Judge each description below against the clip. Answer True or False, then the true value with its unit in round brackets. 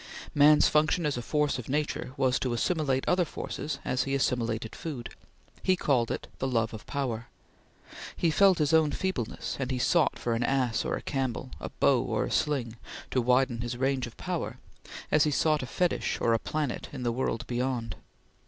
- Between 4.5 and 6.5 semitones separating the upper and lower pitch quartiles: False (3.9 semitones)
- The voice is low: True (130 Hz)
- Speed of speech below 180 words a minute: False (190 wpm)